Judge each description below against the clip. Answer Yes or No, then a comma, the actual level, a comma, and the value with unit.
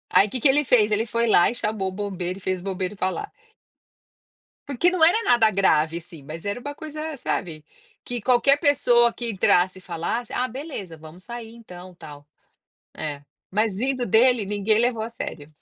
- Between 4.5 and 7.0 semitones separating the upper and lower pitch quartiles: Yes, average, 5.0 semitones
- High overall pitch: Yes, high, 215 Hz